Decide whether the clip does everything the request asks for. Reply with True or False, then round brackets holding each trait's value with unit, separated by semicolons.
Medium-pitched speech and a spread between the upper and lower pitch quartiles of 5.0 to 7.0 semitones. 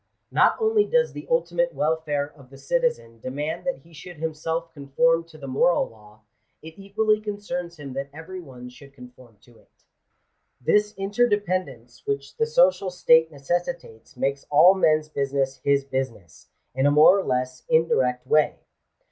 True (155 Hz; 5.4 semitones)